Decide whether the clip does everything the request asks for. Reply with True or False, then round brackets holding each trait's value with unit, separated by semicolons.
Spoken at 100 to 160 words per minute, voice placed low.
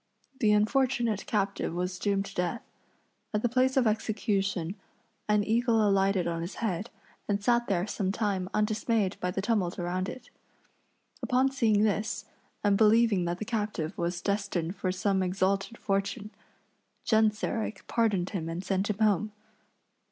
False (150 wpm; 205 Hz)